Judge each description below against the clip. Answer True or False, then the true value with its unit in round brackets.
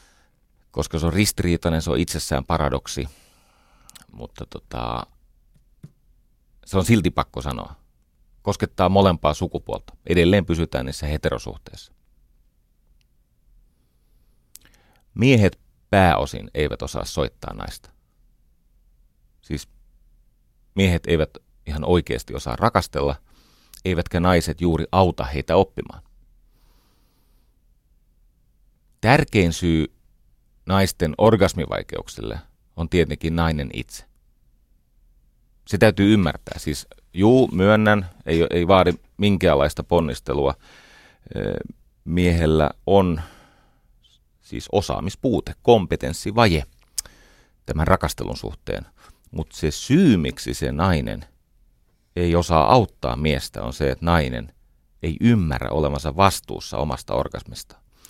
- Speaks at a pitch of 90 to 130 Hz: False (80 Hz)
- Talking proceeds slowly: True (90 wpm)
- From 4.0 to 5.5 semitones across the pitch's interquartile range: True (4.8 semitones)